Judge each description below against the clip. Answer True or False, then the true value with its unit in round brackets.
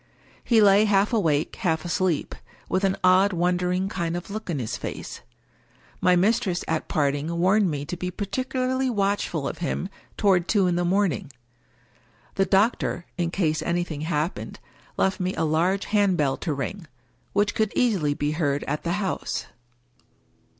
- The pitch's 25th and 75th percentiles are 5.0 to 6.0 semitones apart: False (3.7 semitones)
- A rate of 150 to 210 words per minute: True (160 wpm)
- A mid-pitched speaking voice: True (180 Hz)